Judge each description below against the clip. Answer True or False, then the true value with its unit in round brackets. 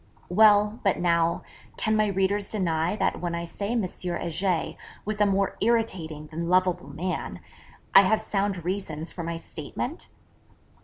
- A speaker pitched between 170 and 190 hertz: True (185 Hz)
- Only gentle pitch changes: False (3.4 semitones)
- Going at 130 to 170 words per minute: True (150 wpm)